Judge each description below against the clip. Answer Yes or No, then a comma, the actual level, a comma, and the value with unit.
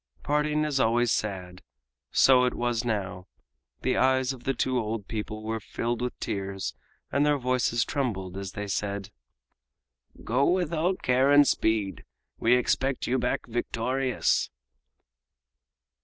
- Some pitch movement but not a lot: Yes, average, 3.8 semitones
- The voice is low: Yes, low, 120 Hz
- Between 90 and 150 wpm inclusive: Yes, average, 140 wpm